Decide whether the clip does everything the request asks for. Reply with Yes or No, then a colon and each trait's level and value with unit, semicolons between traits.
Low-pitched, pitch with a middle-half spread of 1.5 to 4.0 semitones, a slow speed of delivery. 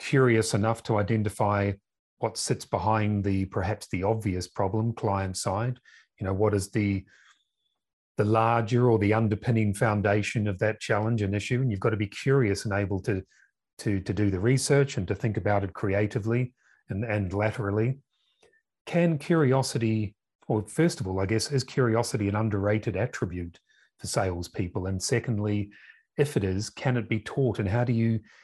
No: low, 110 Hz; average, 3.0 semitones; average, 170 wpm